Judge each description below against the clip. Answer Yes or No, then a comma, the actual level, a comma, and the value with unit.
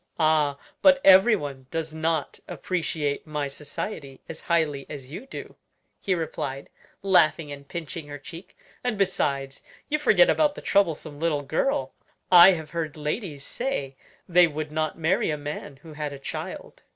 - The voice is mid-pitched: Yes, medium, 155 Hz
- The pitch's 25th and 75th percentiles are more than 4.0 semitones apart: No, average, 3.6 semitones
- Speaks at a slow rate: No, average, 155 wpm